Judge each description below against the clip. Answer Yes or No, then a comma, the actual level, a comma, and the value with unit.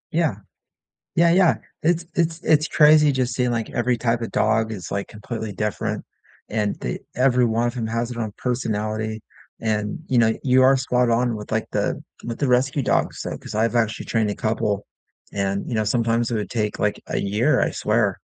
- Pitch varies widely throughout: No, average, 2.7 semitones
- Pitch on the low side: Yes, low, 115 Hz